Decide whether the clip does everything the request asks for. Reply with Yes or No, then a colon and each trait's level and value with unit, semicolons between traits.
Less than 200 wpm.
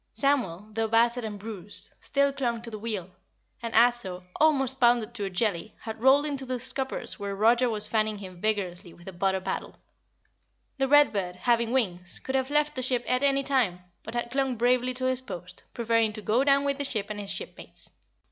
No: fast, 205 wpm